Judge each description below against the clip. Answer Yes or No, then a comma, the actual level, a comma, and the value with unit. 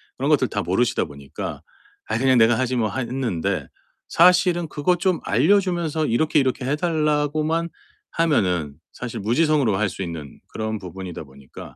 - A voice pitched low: Yes, low, 130 Hz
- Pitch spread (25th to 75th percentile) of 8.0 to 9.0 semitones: Yes, wide, 8.3 semitones